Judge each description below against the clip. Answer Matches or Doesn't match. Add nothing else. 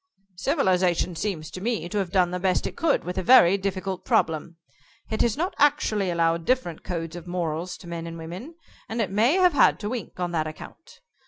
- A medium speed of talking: Doesn't match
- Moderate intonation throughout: Matches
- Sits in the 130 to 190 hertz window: Matches